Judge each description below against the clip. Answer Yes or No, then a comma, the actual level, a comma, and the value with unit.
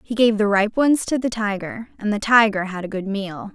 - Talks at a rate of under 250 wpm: No, fast, 255 wpm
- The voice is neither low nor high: No, high, 210 Hz